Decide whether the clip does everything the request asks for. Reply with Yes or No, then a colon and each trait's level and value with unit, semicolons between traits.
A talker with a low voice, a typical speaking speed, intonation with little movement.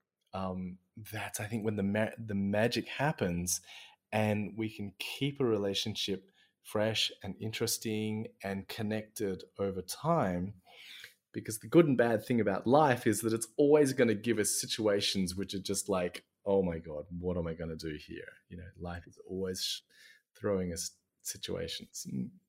No: low, 105 Hz; average, 170 wpm; average, 3.2 semitones